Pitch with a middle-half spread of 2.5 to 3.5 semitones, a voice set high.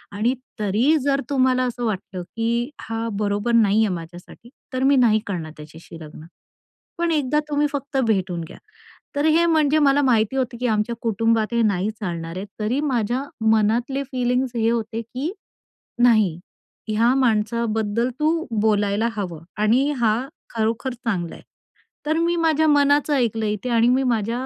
No: average, 4.0 semitones; high, 230 Hz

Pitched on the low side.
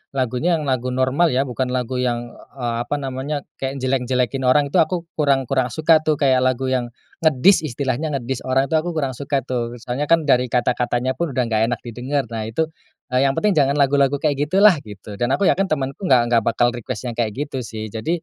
Yes: low, 130 Hz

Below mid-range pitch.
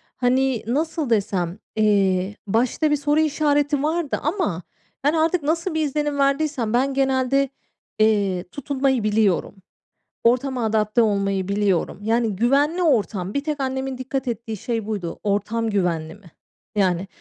No: high, 240 Hz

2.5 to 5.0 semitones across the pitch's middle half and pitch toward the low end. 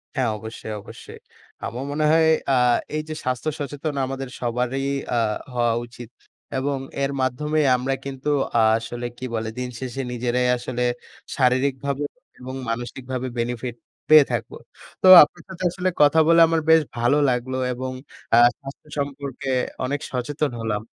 Yes: average, 2.8 semitones; low, 130 Hz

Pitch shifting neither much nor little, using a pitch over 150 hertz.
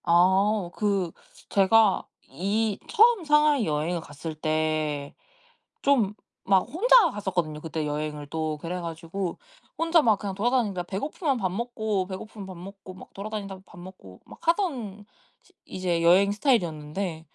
Yes: average, 4.7 semitones; high, 190 Hz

